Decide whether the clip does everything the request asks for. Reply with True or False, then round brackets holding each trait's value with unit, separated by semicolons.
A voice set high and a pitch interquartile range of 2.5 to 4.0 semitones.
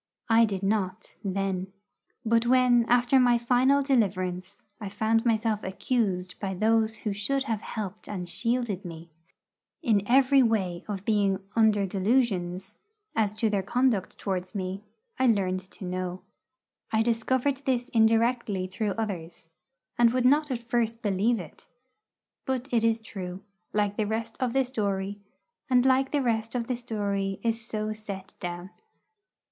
True (220 Hz; 3.7 semitones)